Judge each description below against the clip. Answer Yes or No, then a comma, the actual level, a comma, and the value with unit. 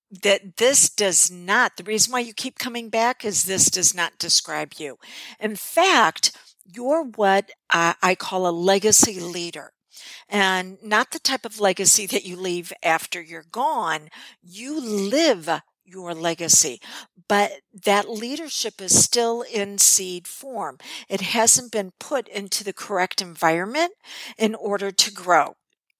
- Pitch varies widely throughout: No, average, 4.2 semitones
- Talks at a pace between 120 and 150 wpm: Yes, average, 145 wpm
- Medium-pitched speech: No, high, 200 Hz